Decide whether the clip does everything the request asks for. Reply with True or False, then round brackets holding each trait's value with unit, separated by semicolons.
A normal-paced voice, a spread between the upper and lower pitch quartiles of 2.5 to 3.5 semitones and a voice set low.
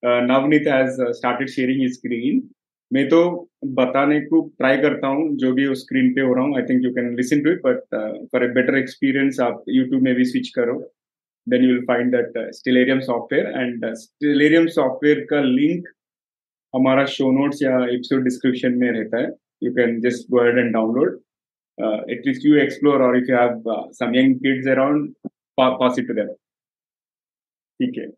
True (165 wpm; 2.9 semitones; 130 Hz)